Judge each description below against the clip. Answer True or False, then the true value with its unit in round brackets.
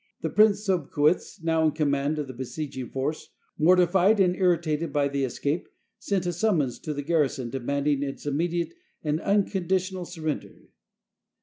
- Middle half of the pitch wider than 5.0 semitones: False (4.1 semitones)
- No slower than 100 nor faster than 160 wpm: True (150 wpm)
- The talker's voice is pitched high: False (160 Hz)